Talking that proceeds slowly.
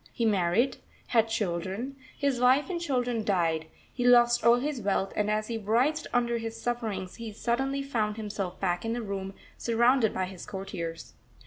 No: average, 175 wpm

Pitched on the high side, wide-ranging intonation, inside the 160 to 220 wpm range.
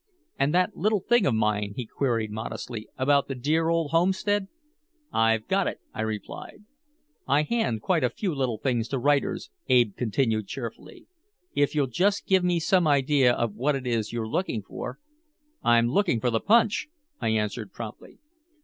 No: low, 135 Hz; wide, 7.0 semitones; average, 175 wpm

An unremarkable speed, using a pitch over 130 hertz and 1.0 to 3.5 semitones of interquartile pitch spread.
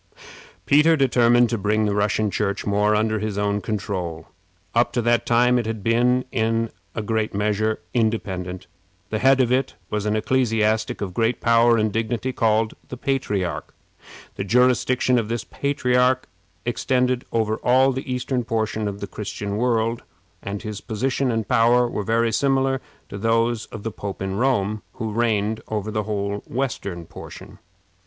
No: average, 160 wpm; low, 110 Hz; average, 2.9 semitones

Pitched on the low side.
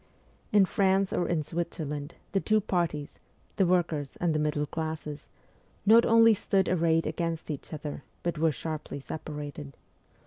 No: medium, 160 Hz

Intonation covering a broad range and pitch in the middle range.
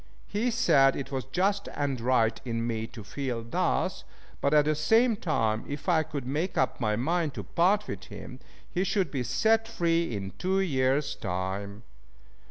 Yes: wide, 7.4 semitones; medium, 145 Hz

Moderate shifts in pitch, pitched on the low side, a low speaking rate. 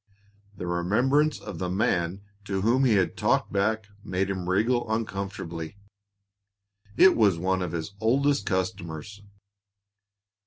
Yes: average, 3.6 semitones; low, 100 Hz; slow, 125 wpm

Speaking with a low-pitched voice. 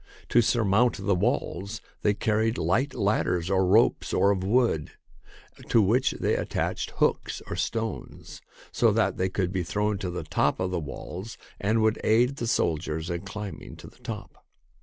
Yes: low, 100 Hz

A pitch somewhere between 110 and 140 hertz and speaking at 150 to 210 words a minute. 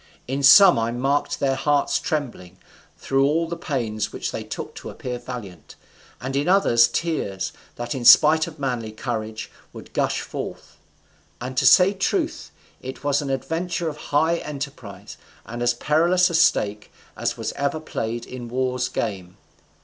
Yes: low, 135 Hz; average, 160 wpm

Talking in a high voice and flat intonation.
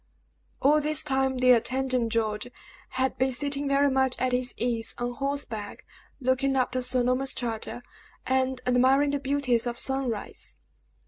Yes: very high, 260 Hz; narrow, 1.8 semitones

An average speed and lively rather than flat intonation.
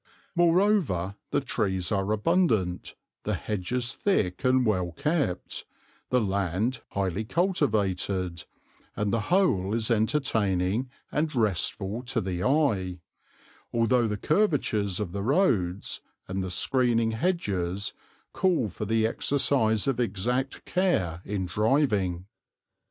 No: slow, 115 wpm; wide, 6.0 semitones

